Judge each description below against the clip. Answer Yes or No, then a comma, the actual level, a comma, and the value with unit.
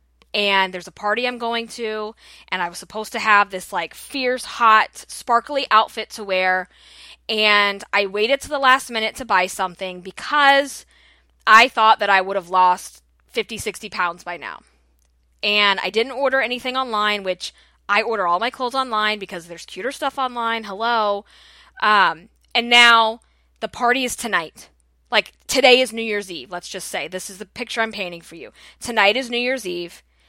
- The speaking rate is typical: Yes, average, 180 wpm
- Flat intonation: No, average, 4.2 semitones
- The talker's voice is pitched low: No, high, 215 Hz